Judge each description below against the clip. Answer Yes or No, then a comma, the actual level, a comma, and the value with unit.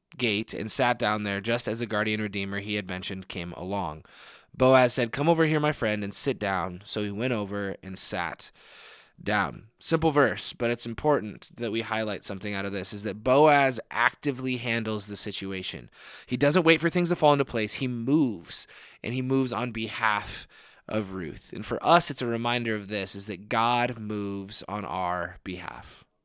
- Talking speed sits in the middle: Yes, average, 190 wpm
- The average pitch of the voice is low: Yes, low, 110 Hz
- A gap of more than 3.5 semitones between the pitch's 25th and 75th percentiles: Yes, average, 4.1 semitones